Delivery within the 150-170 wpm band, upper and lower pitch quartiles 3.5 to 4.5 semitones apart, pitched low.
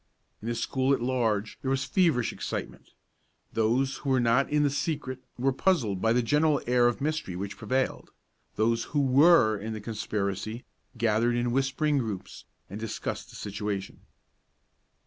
Yes: average, 160 wpm; average, 3.9 semitones; low, 120 Hz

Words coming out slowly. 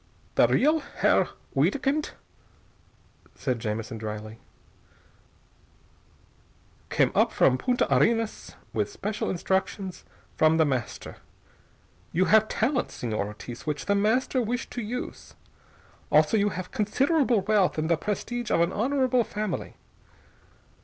Yes: slow, 120 wpm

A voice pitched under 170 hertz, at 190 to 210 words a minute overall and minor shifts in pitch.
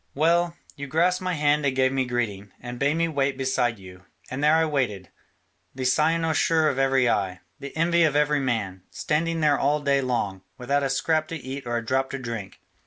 No: low, 135 Hz; fast, 205 wpm; average, 4.1 semitones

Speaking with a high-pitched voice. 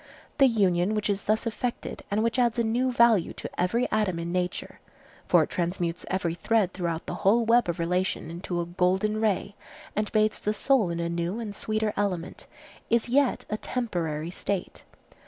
Yes: high, 205 Hz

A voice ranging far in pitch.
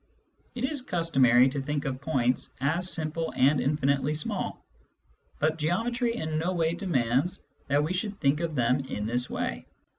No: average, 4.4 semitones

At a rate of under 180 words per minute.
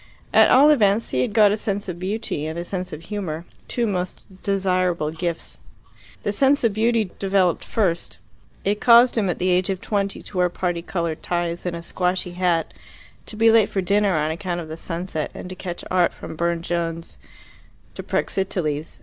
No: average, 190 wpm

